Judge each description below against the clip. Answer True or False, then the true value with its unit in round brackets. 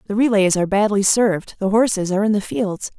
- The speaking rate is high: True (220 wpm)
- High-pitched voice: True (205 Hz)